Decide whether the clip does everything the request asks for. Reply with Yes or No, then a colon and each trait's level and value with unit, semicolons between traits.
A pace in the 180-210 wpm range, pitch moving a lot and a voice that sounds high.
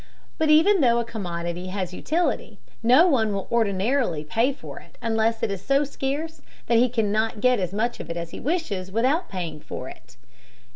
Yes: average, 190 wpm; wide, 6.2 semitones; high, 225 Hz